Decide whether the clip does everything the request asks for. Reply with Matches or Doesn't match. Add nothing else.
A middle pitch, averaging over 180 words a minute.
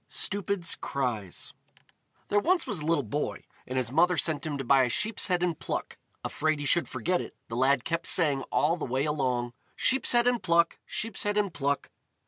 Matches